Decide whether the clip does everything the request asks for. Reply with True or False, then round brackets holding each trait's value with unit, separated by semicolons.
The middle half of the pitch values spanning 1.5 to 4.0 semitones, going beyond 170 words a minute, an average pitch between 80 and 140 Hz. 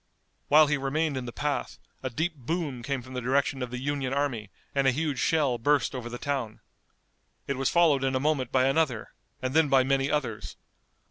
True (2.4 semitones; 205 wpm; 135 Hz)